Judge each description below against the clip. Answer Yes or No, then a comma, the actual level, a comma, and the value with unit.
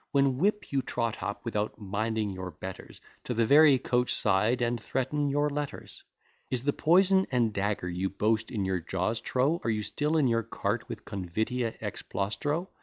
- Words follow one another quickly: No, average, 180 wpm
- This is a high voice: No, low, 115 Hz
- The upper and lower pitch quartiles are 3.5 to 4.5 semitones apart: No, wide, 5.4 semitones